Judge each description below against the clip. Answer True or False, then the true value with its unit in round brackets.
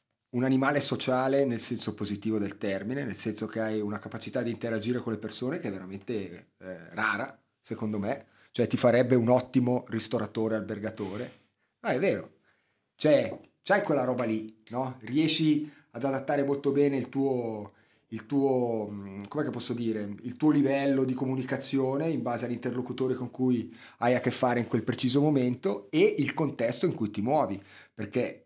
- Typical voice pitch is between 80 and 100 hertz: False (125 Hz)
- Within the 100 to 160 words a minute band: False (170 wpm)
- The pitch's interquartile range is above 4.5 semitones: False (3.2 semitones)